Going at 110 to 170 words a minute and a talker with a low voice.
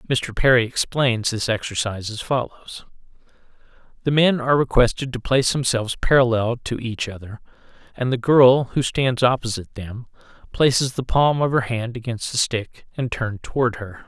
Yes: average, 160 wpm; low, 120 Hz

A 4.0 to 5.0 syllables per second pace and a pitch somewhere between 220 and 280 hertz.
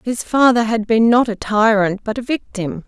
Yes: 4.8 syllables/s; high, 225 Hz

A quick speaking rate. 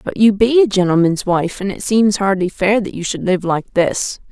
Yes: fast, 235 wpm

